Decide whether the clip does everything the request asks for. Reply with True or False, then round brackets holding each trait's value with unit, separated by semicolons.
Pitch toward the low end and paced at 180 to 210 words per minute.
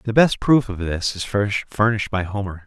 True (105 Hz; 205 wpm)